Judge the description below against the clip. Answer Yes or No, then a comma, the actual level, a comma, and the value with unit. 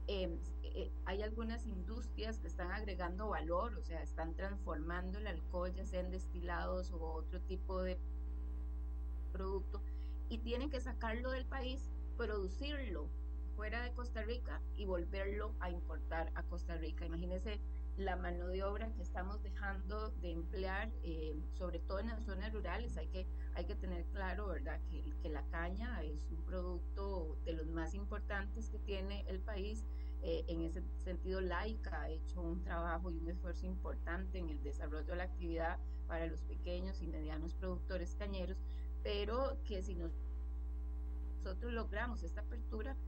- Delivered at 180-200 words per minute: No, average, 160 wpm